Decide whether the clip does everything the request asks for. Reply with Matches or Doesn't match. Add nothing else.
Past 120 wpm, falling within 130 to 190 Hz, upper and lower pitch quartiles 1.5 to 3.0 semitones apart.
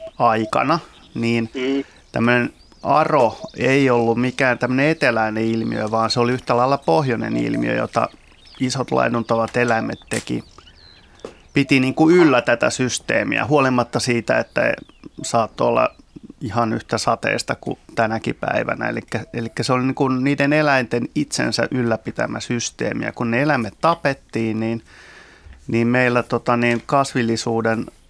Doesn't match